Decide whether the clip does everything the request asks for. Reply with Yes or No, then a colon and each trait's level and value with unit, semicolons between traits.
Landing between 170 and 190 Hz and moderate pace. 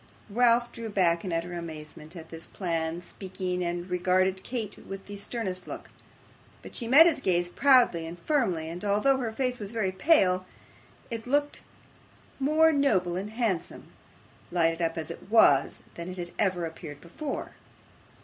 Yes: medium, 185 Hz; average, 160 wpm